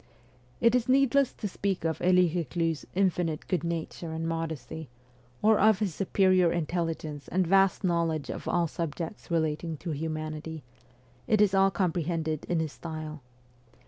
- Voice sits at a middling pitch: Yes, medium, 170 Hz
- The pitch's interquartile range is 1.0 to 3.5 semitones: Yes, average, 2.9 semitones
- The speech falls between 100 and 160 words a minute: Yes, average, 145 wpm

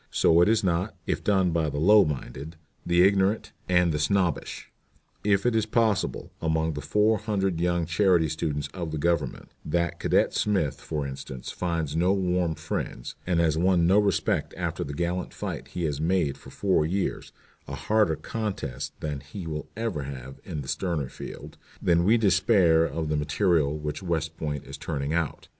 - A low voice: Yes, very low, 85 Hz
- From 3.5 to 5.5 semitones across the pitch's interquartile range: Yes, average, 3.9 semitones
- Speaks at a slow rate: No, average, 180 wpm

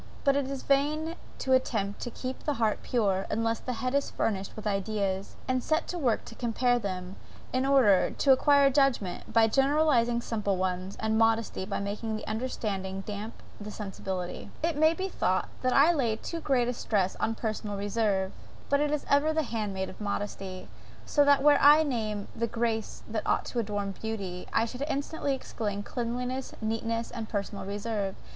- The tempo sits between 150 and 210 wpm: Yes, average, 185 wpm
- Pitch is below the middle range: No, high, 225 Hz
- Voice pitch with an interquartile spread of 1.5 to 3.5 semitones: No, average, 4.8 semitones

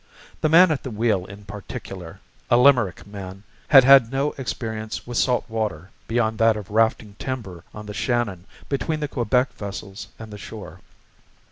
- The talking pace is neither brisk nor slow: Yes, average, 165 wpm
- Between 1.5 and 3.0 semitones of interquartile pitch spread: No, average, 3.7 semitones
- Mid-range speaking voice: No, low, 110 Hz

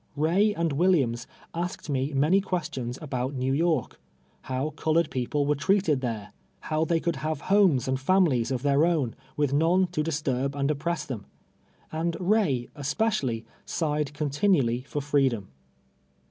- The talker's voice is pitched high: No, medium, 150 Hz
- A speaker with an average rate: Yes, average, 155 wpm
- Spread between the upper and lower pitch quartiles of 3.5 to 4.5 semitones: Yes, average, 4.2 semitones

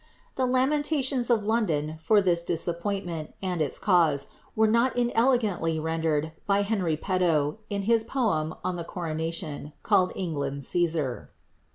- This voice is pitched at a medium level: Yes, medium, 180 Hz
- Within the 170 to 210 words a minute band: No, average, 140 wpm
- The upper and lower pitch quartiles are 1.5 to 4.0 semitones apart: No, wide, 5.6 semitones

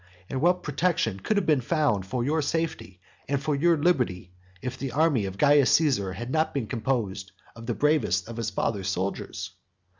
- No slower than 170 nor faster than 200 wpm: Yes, average, 185 wpm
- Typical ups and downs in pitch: No, wide, 7.1 semitones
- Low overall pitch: Yes, low, 130 Hz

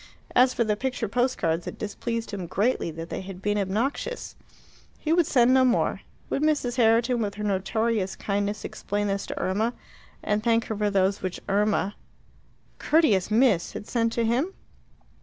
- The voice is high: Yes, high, 215 Hz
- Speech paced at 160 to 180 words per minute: Yes, average, 175 wpm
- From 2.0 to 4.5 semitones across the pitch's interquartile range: Yes, average, 3.5 semitones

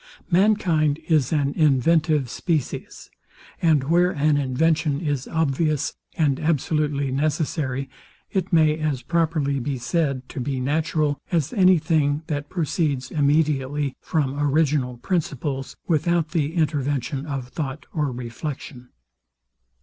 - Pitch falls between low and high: Yes, medium, 150 Hz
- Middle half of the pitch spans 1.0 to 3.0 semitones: Yes, average, 2.7 semitones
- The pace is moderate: No, slow, 120 wpm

